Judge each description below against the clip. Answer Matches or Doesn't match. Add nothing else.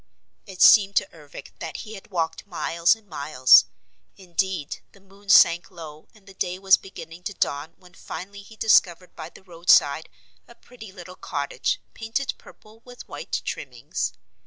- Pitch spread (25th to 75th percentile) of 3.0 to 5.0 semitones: Matches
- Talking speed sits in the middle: Matches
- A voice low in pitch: Doesn't match